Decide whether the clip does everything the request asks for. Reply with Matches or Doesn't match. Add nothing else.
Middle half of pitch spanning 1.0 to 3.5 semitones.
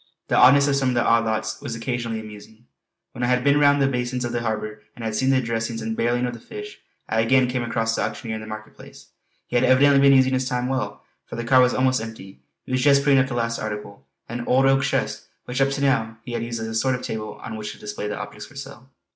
Matches